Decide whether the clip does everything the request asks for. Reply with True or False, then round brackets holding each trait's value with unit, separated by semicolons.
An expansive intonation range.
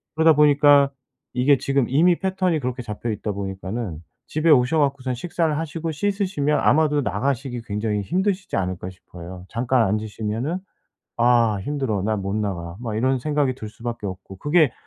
True (6.0 semitones)